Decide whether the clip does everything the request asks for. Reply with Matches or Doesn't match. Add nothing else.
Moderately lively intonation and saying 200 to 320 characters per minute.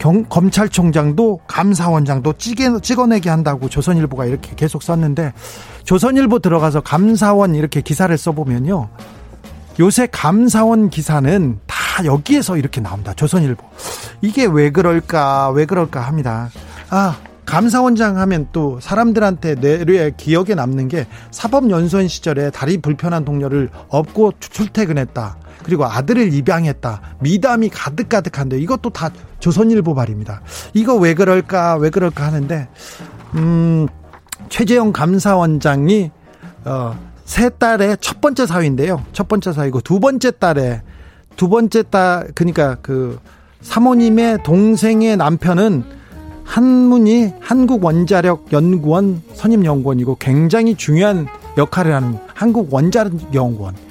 Doesn't match